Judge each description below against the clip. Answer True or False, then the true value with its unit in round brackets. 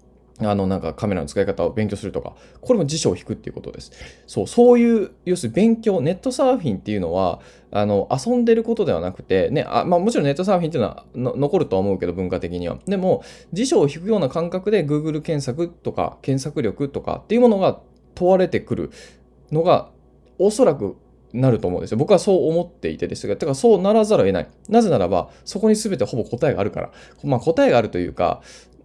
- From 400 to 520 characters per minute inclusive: True (440 characters per minute)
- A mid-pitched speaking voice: True (170 Hz)